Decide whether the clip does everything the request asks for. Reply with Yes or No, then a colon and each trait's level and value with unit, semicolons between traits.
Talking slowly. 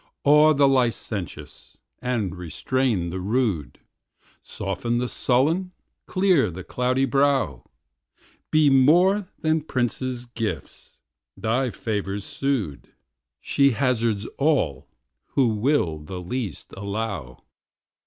Yes: slow, 100 wpm